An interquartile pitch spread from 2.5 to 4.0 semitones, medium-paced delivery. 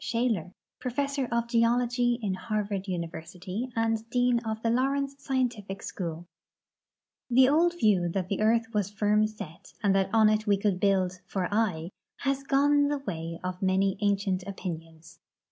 No: average, 4.5 semitones; average, 160 wpm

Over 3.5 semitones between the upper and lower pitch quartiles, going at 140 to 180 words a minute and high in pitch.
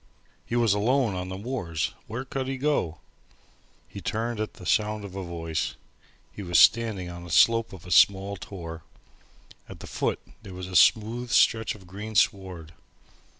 No: average, 4.3 semitones; average, 175 wpm; low, 100 Hz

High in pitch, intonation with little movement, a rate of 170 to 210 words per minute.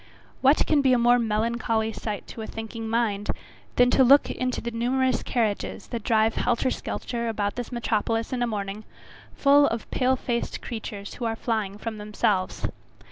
Yes: high, 230 Hz; narrow, 2.3 semitones; average, 175 wpm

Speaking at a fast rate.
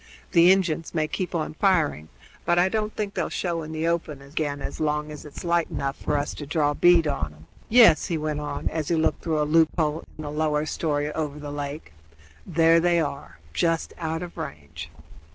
Yes: fast, 210 wpm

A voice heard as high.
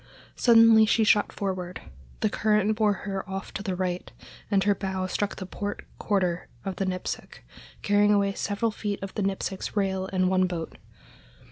Yes: high, 195 Hz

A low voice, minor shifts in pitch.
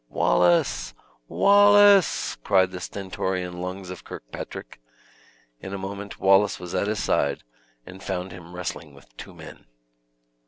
Yes: very low, 95 Hz; narrow, 2.0 semitones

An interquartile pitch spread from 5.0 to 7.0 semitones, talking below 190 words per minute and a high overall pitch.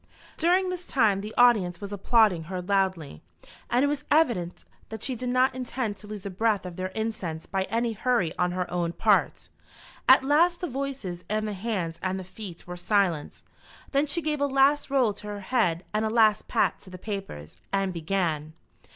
No: wide, 5.6 semitones; average, 195 wpm; high, 210 Hz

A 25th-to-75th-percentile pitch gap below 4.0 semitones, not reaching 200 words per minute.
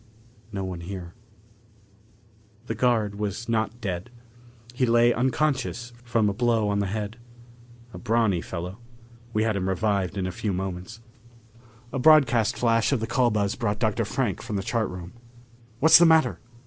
Yes: average, 3.5 semitones; average, 160 wpm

